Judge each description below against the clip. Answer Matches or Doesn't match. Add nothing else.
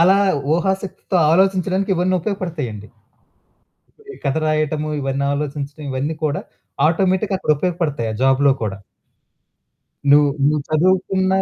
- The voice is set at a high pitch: Doesn't match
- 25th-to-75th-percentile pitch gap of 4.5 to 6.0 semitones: Matches